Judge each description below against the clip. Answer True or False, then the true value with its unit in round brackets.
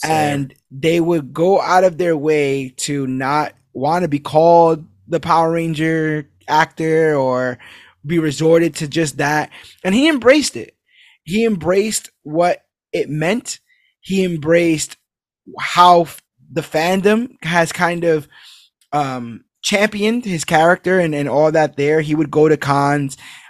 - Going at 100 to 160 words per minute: True (140 wpm)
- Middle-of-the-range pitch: True (160 Hz)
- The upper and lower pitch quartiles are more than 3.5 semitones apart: False (3.1 semitones)